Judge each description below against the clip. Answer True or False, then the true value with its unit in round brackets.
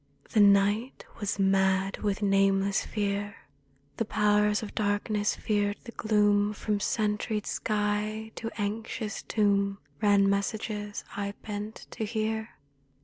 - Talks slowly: True (120 wpm)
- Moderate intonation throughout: False (1.2 semitones)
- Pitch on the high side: True (205 Hz)